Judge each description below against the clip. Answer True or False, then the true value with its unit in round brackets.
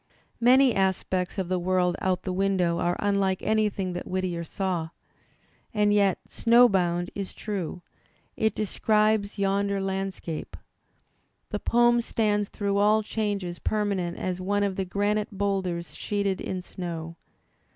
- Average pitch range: False (2.3 semitones)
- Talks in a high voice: True (195 Hz)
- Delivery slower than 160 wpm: True (135 wpm)